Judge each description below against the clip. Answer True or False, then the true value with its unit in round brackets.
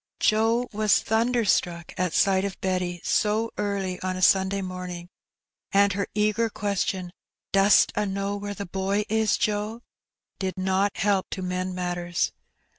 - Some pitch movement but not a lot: False (2.2 semitones)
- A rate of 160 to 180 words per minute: False (145 wpm)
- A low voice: False (195 Hz)